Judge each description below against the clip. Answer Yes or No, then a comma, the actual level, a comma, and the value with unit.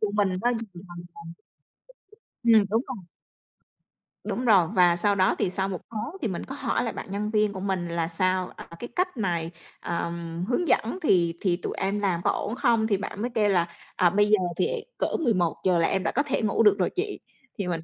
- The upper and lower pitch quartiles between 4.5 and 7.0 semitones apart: No, average, 4.1 semitones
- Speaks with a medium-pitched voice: No, high, 200 Hz